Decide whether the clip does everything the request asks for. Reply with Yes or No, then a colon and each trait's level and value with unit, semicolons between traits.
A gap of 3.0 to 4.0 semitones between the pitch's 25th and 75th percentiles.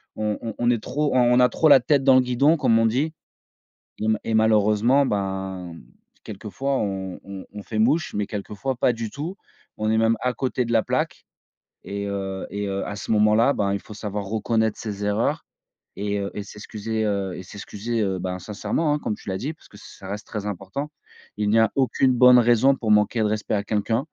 Yes: average, 3.4 semitones